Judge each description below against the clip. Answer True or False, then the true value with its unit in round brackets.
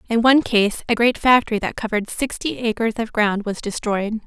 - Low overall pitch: False (225 Hz)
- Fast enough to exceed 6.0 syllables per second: False (5.5 syllables/s)